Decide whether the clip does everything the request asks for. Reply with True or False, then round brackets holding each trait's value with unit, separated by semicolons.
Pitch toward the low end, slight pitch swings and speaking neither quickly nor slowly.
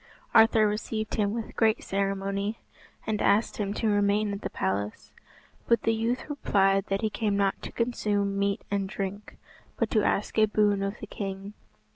False (205 Hz; 1.7 semitones; 175 wpm)